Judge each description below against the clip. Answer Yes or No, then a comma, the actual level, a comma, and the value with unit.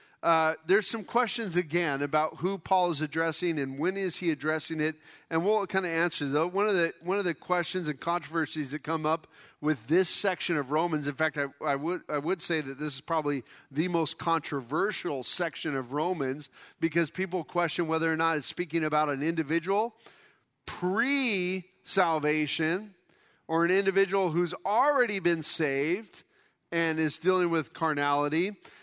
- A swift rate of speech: No, average, 170 wpm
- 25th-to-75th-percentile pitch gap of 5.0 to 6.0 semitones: No, average, 3.0 semitones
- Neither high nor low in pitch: Yes, medium, 165 Hz